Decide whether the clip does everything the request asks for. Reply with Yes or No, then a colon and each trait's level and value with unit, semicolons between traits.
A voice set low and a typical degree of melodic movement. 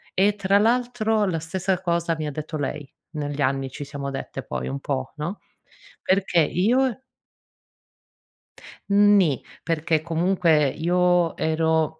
No: medium, 165 Hz; average, 4.3 semitones